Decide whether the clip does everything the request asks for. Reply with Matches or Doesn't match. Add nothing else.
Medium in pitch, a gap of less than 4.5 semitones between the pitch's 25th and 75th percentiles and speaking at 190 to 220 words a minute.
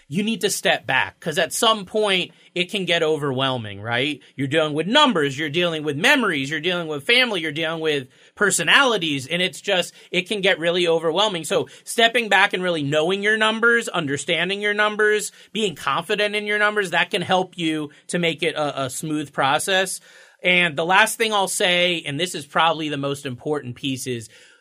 Doesn't match